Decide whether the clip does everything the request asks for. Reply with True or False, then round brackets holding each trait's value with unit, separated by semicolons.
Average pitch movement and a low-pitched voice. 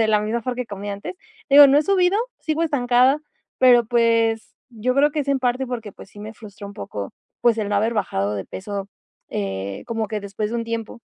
False (3.7 semitones; 230 Hz)